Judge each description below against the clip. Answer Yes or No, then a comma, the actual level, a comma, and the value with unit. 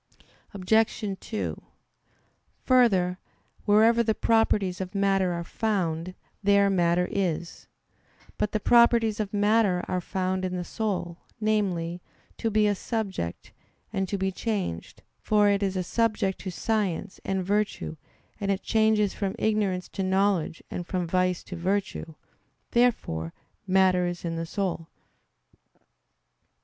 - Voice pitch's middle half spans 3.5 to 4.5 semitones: No, average, 2.9 semitones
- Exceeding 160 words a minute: No, slow, 135 wpm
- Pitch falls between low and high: No, high, 195 Hz